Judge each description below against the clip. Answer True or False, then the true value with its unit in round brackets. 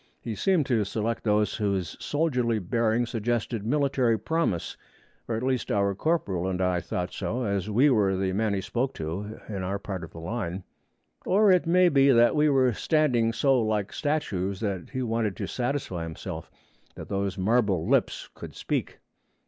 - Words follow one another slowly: False (175 wpm)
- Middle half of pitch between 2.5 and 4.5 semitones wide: False (5.0 semitones)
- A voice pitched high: False (110 Hz)